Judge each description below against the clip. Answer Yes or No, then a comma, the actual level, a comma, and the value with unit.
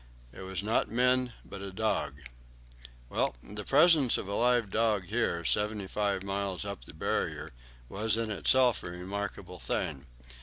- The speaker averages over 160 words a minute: No, average, 155 wpm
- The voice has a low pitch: Yes, low, 105 Hz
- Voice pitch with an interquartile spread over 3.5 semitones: No, average, 3.2 semitones